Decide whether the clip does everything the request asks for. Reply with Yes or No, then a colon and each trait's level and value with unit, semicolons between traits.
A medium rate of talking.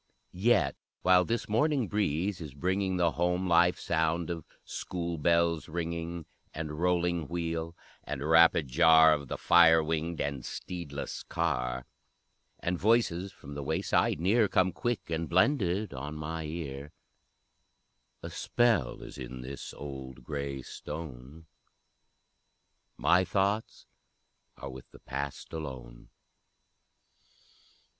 No: slow, 120 wpm